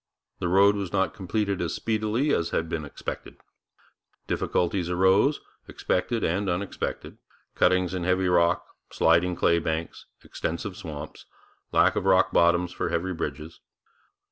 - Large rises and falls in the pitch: No, narrow, 2.5 semitones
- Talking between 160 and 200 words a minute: No, slow, 135 wpm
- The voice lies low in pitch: Yes, very low, 90 Hz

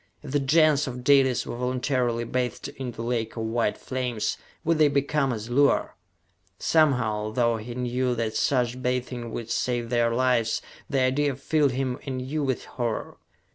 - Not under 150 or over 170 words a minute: Yes, average, 165 wpm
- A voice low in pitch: Yes, low, 125 Hz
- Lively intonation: No, narrow, 2.5 semitones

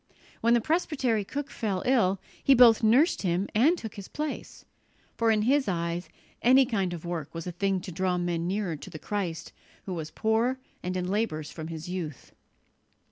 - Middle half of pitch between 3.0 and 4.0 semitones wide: No, average, 5.2 semitones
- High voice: Yes, high, 195 Hz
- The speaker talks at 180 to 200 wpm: Yes, average, 190 wpm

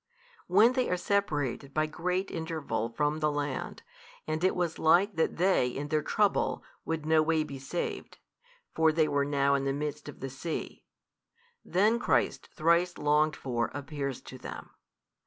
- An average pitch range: Yes, average, 3.4 semitones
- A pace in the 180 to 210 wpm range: No, average, 165 wpm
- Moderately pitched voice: Yes, medium, 155 Hz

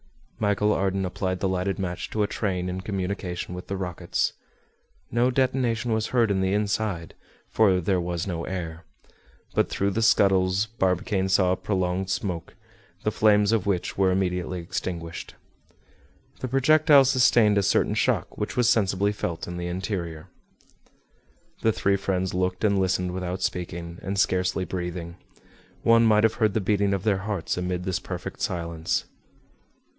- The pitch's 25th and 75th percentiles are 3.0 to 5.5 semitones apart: No, narrow, 2.6 semitones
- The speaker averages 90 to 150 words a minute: No, average, 160 wpm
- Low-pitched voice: Yes, very low, 95 Hz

